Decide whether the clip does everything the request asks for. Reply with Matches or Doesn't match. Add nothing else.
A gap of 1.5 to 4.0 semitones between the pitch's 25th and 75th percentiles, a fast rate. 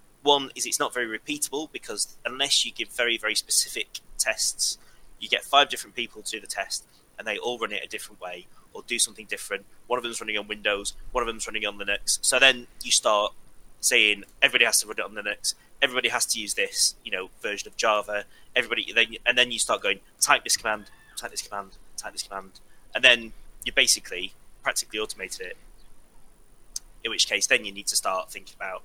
Doesn't match